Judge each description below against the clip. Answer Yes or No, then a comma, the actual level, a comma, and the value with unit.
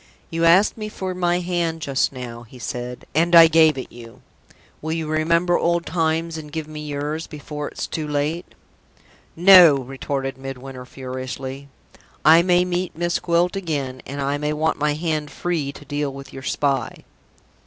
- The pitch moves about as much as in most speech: Yes, average, 3.7 semitones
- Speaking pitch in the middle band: Yes, medium, 150 Hz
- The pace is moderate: Yes, average, 170 wpm